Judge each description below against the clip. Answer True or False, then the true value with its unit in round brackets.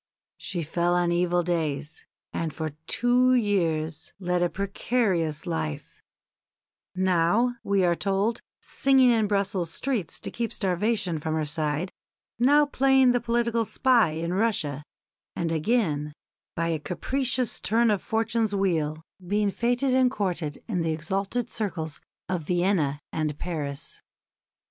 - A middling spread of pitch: False (6.1 semitones)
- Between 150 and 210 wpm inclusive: False (135 wpm)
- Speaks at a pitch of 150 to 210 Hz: True (185 Hz)